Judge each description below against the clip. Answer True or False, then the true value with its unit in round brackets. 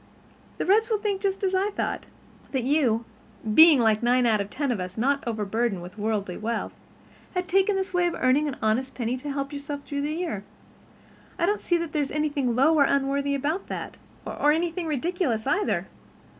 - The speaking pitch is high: True (280 Hz)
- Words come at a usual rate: True (190 wpm)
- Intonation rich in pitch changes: True (6.4 semitones)